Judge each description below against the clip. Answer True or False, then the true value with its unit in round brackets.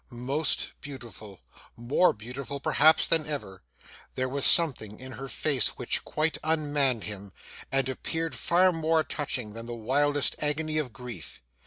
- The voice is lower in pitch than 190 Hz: True (135 Hz)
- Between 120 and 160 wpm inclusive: True (145 wpm)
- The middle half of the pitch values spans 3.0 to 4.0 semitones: False (4.5 semitones)